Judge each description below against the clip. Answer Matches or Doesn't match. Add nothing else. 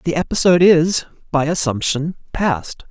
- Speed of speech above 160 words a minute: Doesn't match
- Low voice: Doesn't match